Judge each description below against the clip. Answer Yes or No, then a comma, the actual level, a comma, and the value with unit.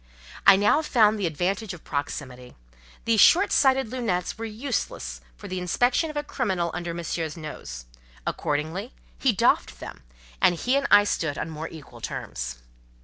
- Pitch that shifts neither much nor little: No, wide, 7.1 semitones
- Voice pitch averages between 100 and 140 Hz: No, medium, 180 Hz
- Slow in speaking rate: No, average, 160 wpm